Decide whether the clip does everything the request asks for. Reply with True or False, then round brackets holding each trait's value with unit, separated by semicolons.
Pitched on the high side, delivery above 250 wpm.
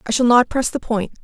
True (240 Hz; 295 wpm)